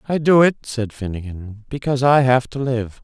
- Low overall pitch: Yes, low, 125 Hz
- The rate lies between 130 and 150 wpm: No, average, 200 wpm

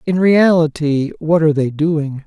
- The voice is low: No, medium, 160 Hz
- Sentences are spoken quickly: No, average, 160 wpm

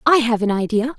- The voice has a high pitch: Yes, high, 240 Hz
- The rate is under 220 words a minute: No, fast, 245 wpm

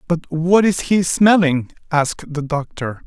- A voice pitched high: No, medium, 165 Hz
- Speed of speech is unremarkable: Yes, average, 155 wpm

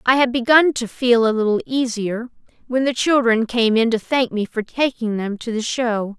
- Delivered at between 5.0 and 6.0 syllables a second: No, 4.8 syllables/s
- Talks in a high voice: Yes, high, 240 Hz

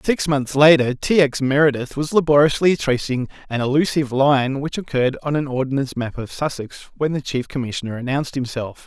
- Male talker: Yes, male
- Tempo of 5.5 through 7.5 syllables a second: Yes, 5.7 syllables/s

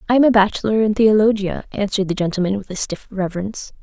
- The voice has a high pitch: Yes, high, 205 Hz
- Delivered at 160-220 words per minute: Yes, fast, 205 wpm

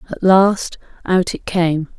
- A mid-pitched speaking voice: Yes, medium, 180 Hz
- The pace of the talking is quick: No, average, 150 wpm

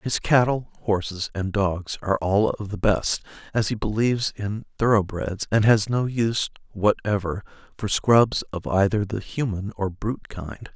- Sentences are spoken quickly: No, average, 160 wpm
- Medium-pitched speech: No, low, 105 Hz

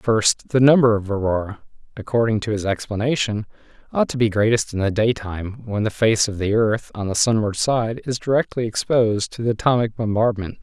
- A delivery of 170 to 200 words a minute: Yes, average, 185 wpm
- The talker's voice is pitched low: Yes, low, 110 Hz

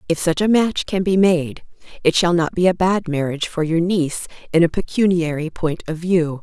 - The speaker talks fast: Yes, fast, 215 wpm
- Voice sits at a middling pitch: Yes, medium, 170 Hz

